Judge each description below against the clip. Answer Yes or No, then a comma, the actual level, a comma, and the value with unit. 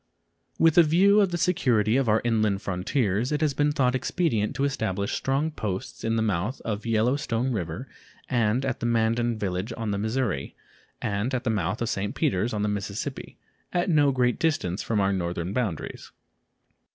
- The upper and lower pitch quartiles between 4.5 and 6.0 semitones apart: Yes, average, 4.8 semitones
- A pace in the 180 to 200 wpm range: Yes, average, 185 wpm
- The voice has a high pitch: No, low, 115 Hz